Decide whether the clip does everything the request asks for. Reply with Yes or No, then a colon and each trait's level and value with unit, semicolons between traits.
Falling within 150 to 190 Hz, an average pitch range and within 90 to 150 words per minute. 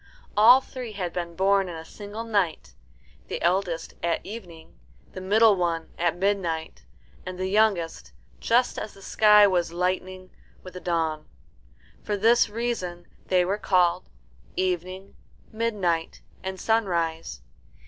Yes: medium, 185 Hz; average, 3.3 semitones; slow, 135 wpm